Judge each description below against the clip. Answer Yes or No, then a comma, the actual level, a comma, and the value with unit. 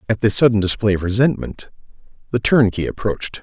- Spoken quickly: No, average, 160 wpm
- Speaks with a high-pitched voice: No, low, 110 Hz